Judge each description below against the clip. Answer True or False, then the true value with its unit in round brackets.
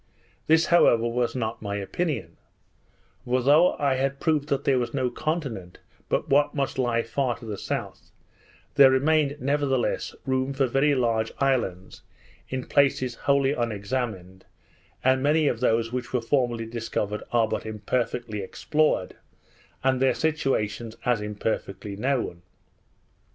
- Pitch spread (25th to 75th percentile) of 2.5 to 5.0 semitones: True (3.5 semitones)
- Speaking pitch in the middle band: False (125 Hz)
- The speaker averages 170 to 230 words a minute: False (140 wpm)